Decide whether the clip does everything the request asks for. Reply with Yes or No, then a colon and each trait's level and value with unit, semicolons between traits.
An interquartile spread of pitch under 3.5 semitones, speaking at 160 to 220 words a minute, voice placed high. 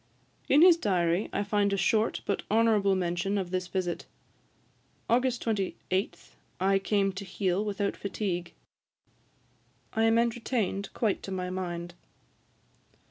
No: average, 2.9 semitones; slow, 135 wpm; high, 200 Hz